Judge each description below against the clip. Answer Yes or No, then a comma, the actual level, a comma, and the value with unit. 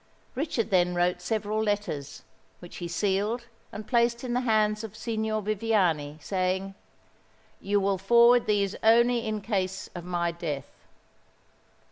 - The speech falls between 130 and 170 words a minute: Yes, slow, 135 wpm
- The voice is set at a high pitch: Yes, high, 205 Hz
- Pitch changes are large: No, average, 3.7 semitones